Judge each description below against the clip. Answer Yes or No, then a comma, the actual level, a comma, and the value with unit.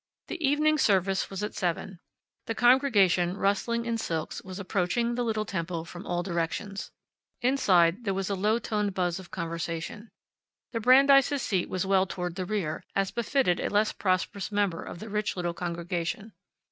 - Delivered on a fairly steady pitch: No, average, 4.3 semitones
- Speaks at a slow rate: No, average, 170 wpm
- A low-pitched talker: No, high, 195 Hz